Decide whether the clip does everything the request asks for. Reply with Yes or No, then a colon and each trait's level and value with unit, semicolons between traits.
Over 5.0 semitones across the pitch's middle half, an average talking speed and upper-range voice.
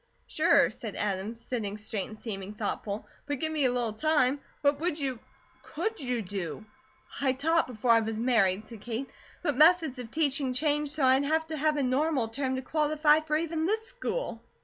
Yes: wide, 5.4 semitones; average, 195 wpm; very high, 265 Hz